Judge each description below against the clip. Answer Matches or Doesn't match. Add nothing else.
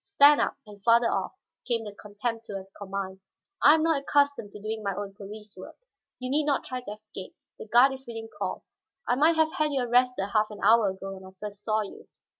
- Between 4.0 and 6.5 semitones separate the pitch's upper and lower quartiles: Matches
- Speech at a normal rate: Doesn't match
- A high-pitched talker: Matches